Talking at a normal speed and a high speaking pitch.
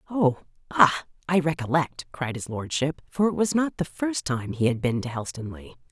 No: average, 185 wpm; medium, 145 Hz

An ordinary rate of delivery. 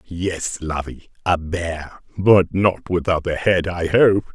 Yes: average, 150 wpm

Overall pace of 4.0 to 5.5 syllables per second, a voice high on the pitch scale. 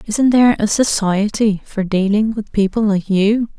Yes: 4.5 syllables/s; high, 210 Hz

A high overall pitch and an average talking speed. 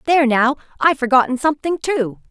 Yes: very high, 275 Hz; average, 155 wpm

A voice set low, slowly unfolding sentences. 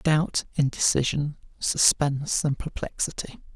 No: medium, 145 Hz; slow, 85 wpm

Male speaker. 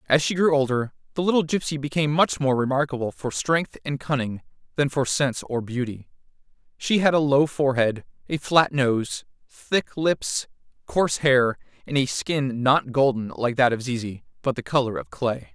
Yes: male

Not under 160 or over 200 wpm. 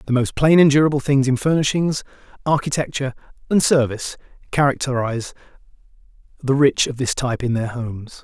No: average, 145 wpm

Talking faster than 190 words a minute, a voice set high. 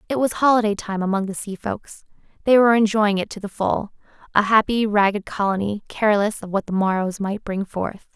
Yes: average, 200 wpm; high, 205 Hz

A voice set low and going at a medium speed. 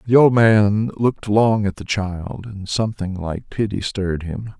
Yes: low, 105 Hz; average, 185 wpm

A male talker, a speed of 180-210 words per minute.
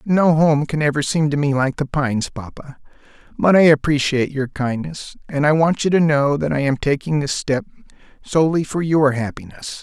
Yes: male; average, 195 wpm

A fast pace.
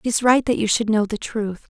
Yes: fast, 310 wpm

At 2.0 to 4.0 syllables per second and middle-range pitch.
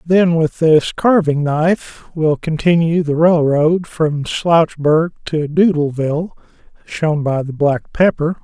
Yes: 3.7 syllables/s; medium, 160 Hz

